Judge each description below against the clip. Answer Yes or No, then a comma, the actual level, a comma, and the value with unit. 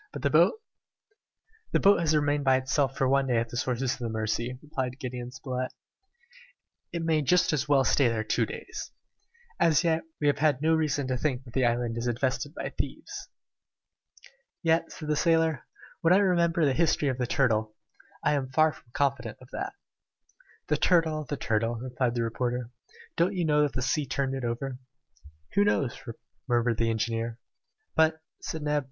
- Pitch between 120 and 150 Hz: Yes, low, 135 Hz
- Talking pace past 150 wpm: Yes, average, 185 wpm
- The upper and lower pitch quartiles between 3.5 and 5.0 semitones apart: Yes, average, 4.2 semitones